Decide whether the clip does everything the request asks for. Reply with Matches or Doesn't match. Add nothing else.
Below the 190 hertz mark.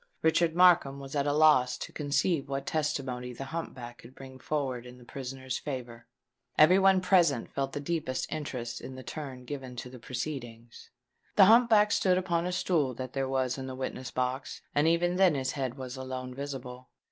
Matches